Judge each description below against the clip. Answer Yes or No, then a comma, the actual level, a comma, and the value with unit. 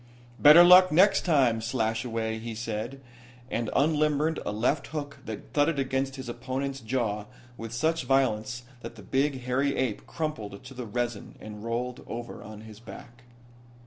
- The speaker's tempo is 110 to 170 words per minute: Yes, average, 155 wpm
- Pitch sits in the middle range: No, low, 125 Hz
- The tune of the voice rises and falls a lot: No, average, 3.8 semitones